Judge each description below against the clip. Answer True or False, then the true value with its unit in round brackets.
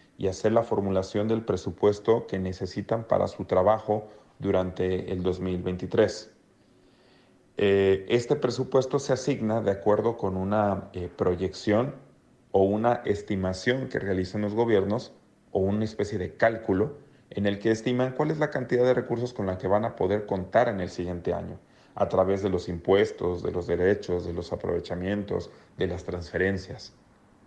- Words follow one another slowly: False (155 wpm)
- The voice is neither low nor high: False (105 Hz)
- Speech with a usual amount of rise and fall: True (4.0 semitones)